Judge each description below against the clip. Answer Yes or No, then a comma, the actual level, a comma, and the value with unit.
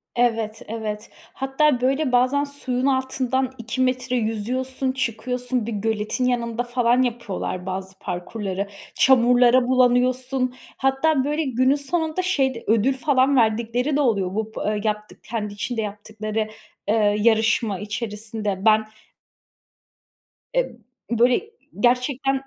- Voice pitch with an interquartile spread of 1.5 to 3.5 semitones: Yes, average, 3.2 semitones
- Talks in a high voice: Yes, high, 245 Hz